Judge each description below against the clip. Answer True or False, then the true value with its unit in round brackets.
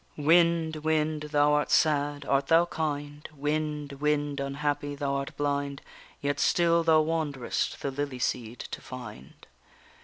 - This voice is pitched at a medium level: True (145 Hz)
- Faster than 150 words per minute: False (135 wpm)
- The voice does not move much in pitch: True (1.8 semitones)